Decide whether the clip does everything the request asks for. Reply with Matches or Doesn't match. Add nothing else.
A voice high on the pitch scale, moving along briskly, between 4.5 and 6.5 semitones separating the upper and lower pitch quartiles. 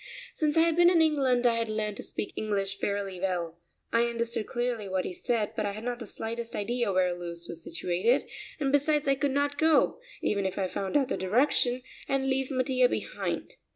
Matches